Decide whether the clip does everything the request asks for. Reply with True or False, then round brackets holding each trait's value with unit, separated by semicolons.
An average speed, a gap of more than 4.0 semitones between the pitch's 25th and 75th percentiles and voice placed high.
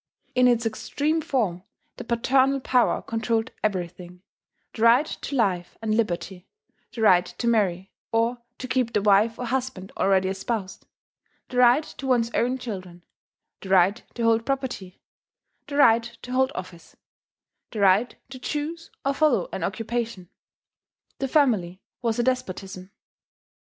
True (145 wpm; 5.0 semitones; 230 Hz)